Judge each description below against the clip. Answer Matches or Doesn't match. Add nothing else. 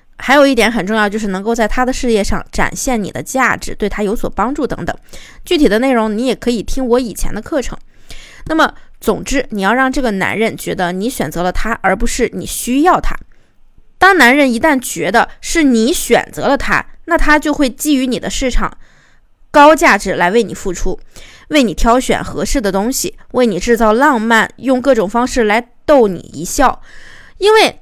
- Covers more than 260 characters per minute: Matches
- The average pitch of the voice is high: Matches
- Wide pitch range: Doesn't match